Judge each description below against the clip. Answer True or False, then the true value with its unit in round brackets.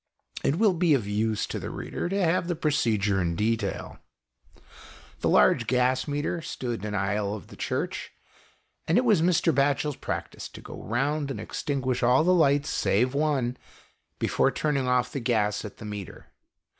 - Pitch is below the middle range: True (130 Hz)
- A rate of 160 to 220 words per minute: True (175 wpm)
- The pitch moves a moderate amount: False (6.1 semitones)